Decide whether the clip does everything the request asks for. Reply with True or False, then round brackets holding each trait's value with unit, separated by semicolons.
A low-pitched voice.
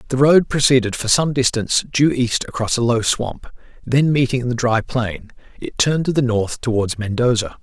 True (125 Hz)